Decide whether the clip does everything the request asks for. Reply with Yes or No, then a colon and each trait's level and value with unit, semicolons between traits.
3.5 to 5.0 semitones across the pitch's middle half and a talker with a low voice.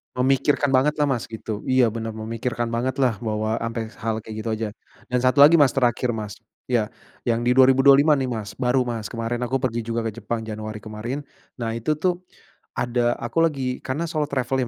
No: average, 2.9 semitones; low, 120 Hz